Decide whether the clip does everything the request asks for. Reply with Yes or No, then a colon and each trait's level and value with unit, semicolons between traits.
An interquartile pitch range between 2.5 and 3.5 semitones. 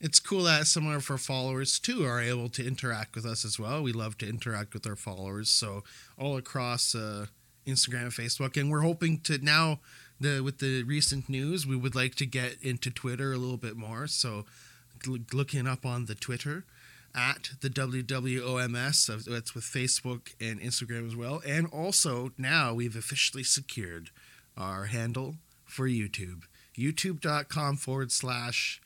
Yes: average, 3.0 semitones